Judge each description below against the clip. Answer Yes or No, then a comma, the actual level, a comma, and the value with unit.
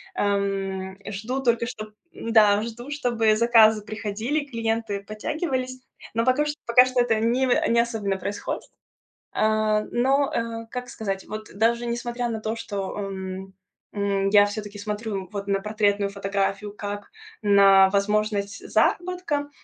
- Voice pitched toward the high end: Yes, high, 215 Hz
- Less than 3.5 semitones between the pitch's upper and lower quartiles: Yes, average, 3.0 semitones